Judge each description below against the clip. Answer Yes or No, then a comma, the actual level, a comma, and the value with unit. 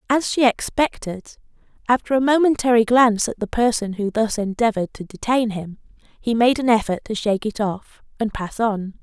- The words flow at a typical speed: Yes, average, 180 wpm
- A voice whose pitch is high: Yes, high, 225 Hz